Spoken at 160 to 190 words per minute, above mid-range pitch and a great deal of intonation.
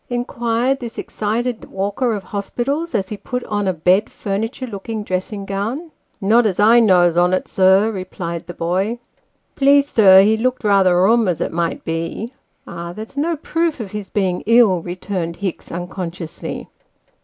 No: average, 170 wpm; high, 205 Hz; average, 4.3 semitones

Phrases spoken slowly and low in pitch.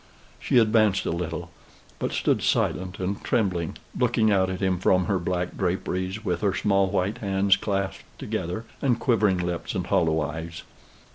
No: average, 160 wpm; very low, 95 Hz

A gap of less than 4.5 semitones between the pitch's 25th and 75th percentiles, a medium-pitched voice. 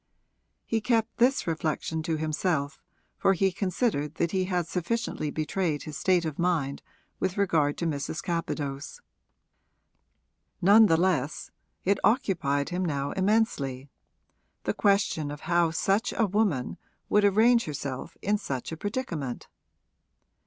No: average, 5.1 semitones; medium, 170 Hz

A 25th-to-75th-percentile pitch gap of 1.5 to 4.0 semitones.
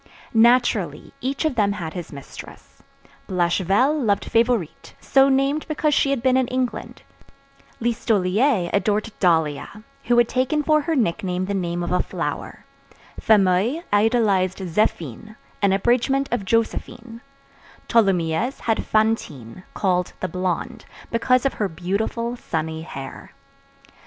No: wide, 5.4 semitones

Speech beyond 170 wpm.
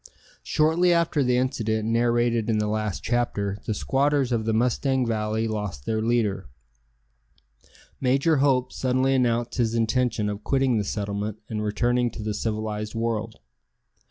No: average, 145 wpm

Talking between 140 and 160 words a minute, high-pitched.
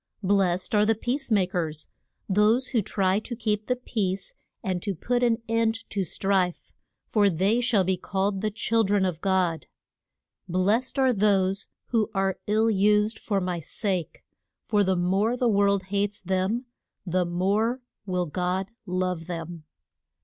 Yes: average, 155 wpm; high, 200 Hz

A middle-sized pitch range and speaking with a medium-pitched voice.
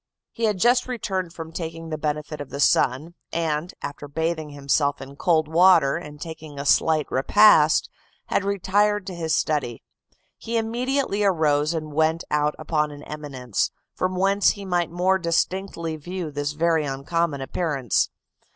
Yes: average, 3.9 semitones; medium, 160 Hz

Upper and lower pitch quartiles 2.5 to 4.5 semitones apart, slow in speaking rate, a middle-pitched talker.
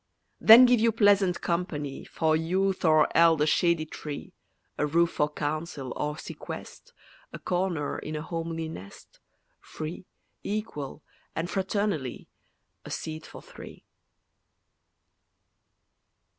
Yes: average, 3.6 semitones; slow, 115 wpm; medium, 165 Hz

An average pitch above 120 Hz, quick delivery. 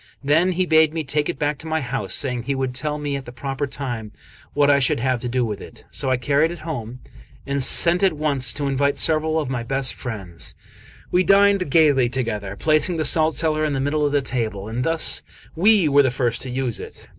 Yes: medium, 140 Hz; fast, 230 wpm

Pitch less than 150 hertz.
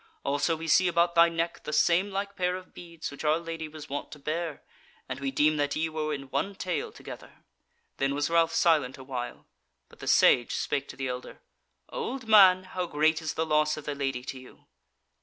No: medium, 155 Hz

